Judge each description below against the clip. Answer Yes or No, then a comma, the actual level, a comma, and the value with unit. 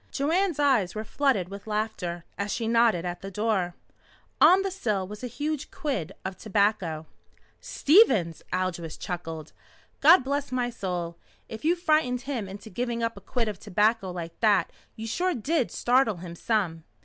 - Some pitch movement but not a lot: No, wide, 6.3 semitones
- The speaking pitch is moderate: No, high, 215 Hz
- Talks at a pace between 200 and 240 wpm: No, average, 165 wpm